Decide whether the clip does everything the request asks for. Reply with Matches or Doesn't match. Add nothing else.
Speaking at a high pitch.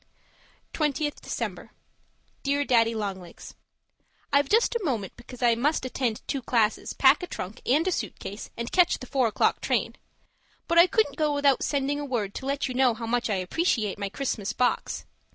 Matches